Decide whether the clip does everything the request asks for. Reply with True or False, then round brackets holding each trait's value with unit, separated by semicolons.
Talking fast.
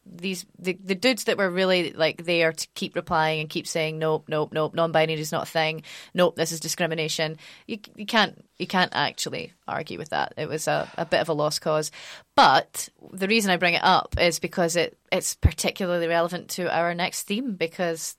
True (210 wpm)